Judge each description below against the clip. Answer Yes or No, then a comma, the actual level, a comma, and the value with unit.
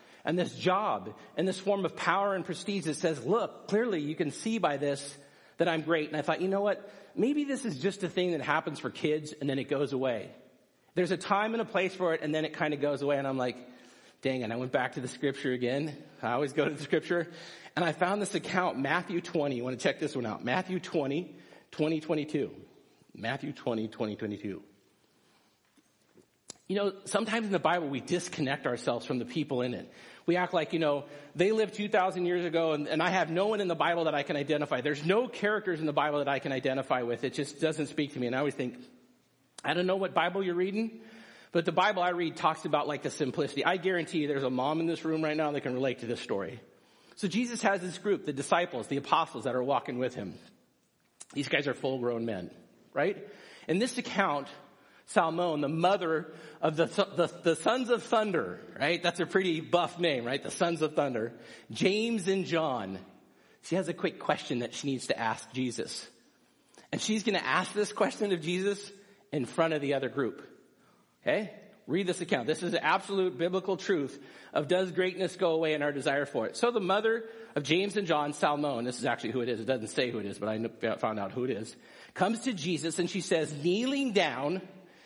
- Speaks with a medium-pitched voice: Yes, medium, 165 Hz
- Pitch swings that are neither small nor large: Yes, average, 4.9 semitones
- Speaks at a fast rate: Yes, fast, 225 wpm